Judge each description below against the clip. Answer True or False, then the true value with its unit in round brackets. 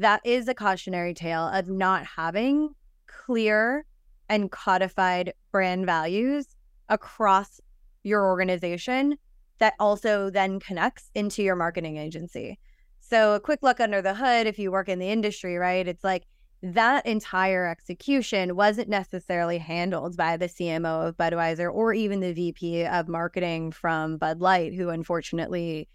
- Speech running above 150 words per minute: False (145 wpm)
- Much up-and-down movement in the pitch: False (3.7 semitones)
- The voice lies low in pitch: False (190 Hz)